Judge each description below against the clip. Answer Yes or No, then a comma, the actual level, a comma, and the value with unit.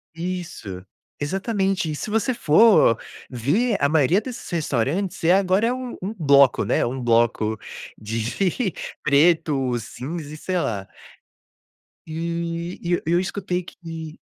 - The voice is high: No, medium, 165 Hz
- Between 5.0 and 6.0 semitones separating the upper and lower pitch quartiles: Yes, wide, 5.5 semitones